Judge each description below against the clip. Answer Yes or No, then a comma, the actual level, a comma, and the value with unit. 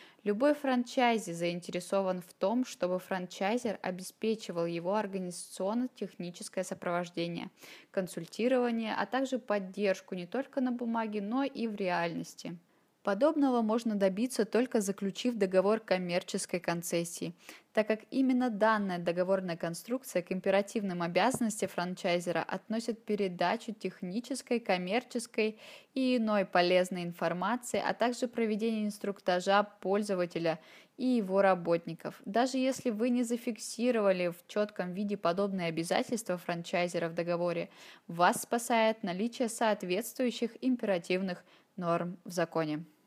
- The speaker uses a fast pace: No, slow, 110 wpm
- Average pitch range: Yes, average, 4.6 semitones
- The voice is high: Yes, high, 200 Hz